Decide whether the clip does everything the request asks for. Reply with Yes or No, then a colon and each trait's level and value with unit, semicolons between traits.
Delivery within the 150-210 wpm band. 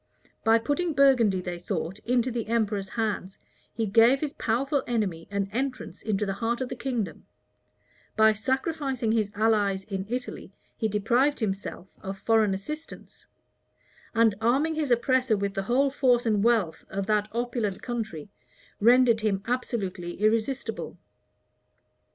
No: average, 140 wpm